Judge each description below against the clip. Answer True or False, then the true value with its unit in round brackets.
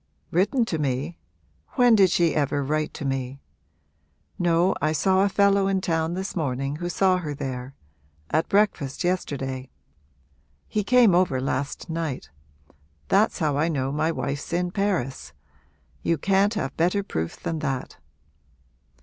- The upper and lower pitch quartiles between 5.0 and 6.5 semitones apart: True (5.5 semitones)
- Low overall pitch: False (160 Hz)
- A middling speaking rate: True (145 wpm)